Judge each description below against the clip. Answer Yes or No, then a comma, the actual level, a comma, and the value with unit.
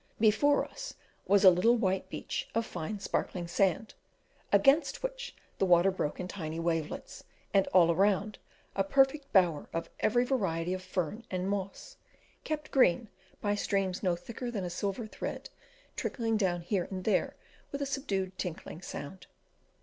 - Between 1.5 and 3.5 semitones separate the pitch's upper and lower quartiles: No, average, 4.4 semitones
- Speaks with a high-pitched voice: Yes, high, 195 Hz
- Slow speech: No, average, 155 wpm